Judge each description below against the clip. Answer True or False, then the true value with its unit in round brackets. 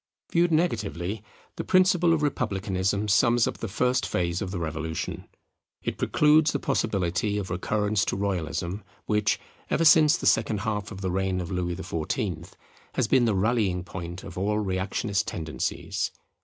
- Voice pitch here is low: True (100 Hz)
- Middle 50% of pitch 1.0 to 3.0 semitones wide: False (4.0 semitones)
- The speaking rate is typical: True (155 wpm)